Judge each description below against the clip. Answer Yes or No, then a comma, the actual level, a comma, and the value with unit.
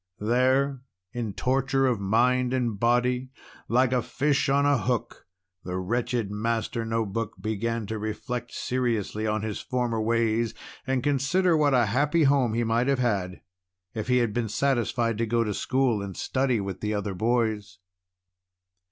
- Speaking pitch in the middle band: No, low, 120 Hz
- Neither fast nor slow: Yes, average, 165 wpm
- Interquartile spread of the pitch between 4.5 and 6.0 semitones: No, average, 2.9 semitones